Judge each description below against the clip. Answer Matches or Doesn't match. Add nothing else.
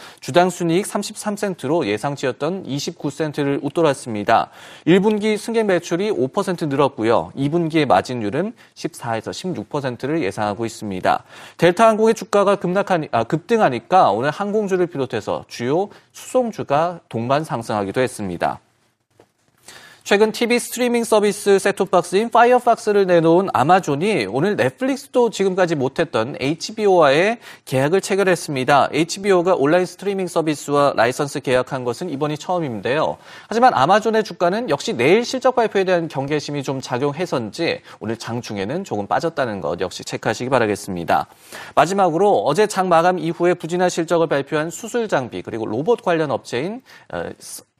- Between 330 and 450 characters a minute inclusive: Matches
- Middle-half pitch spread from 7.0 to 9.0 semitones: Doesn't match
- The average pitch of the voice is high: Doesn't match